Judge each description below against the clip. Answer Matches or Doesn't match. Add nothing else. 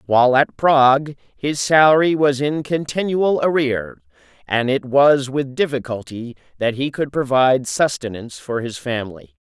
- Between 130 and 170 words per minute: Matches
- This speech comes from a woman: Doesn't match